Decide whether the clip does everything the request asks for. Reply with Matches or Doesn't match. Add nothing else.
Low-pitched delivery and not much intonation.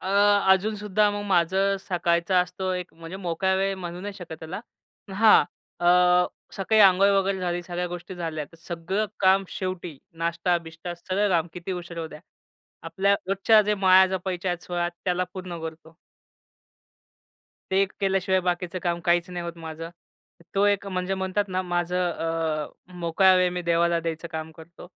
Doesn't match